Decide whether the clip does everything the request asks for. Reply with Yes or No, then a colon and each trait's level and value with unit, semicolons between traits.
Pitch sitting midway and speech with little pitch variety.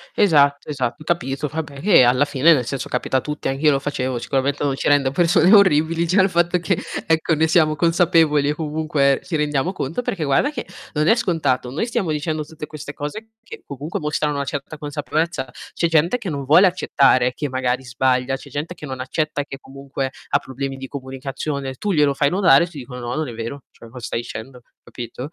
No: medium, 145 Hz; average, 3.4 semitones